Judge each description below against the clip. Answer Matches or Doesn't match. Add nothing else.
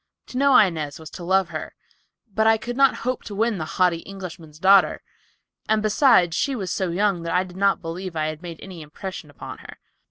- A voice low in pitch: Doesn't match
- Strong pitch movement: Doesn't match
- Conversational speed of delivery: Doesn't match